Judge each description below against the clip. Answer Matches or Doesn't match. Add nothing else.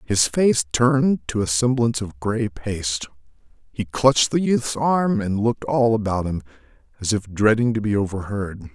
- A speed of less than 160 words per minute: Doesn't match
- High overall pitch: Doesn't match